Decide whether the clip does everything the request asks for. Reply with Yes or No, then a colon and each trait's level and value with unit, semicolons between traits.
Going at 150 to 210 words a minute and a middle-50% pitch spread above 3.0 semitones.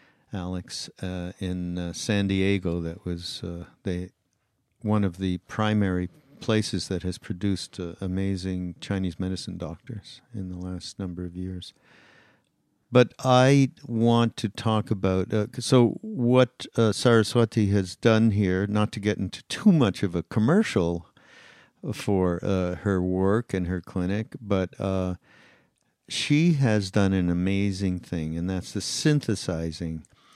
No: average, 140 wpm; average, 3.6 semitones